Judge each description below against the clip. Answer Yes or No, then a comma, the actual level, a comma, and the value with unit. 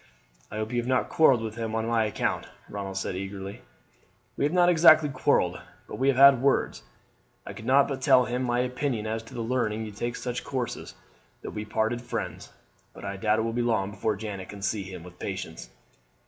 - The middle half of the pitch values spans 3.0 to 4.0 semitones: Yes, average, 3.6 semitones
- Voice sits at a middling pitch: No, low, 115 Hz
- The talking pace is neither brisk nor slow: No, fast, 215 wpm